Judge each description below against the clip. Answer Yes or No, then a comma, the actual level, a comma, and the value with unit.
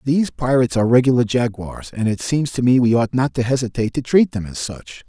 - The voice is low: Yes, low, 120 Hz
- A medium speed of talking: No, fast, 235 wpm